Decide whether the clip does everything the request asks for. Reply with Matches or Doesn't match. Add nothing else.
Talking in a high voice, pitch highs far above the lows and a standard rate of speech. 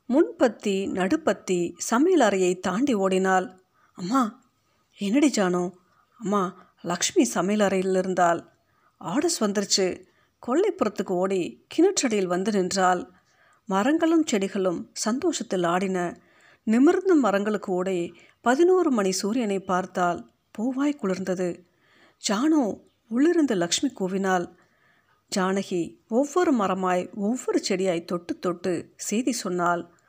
Matches